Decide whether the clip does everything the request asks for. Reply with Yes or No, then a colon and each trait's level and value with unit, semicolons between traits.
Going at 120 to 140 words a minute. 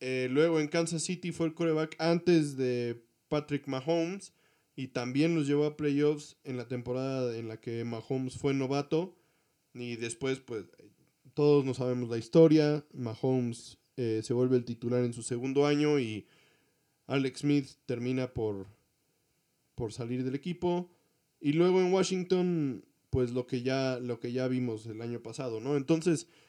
No: average, 160 wpm